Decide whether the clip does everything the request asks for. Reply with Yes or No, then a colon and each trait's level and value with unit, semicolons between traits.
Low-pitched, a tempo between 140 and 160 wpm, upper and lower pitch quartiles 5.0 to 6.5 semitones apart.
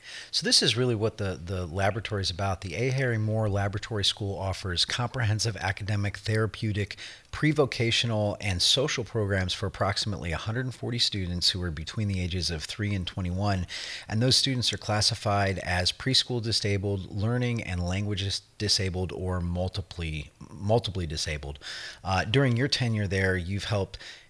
No: low, 100 Hz; average, 150 wpm; average, 3.7 semitones